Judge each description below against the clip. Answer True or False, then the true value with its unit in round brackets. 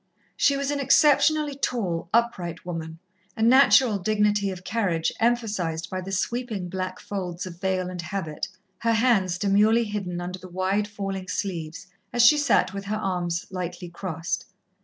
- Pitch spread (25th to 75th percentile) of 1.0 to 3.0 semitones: False (4.2 semitones)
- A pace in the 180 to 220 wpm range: False (155 wpm)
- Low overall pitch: False (195 Hz)